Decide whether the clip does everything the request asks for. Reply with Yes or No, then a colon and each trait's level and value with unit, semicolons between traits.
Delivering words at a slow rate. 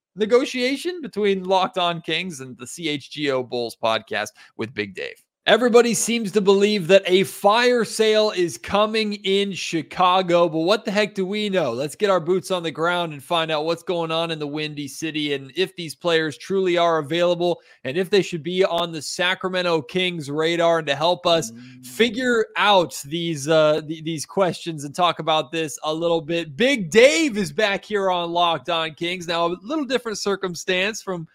No: average, 190 wpm